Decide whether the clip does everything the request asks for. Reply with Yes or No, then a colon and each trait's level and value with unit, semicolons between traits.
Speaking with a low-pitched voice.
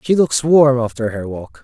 Yes: low, 120 Hz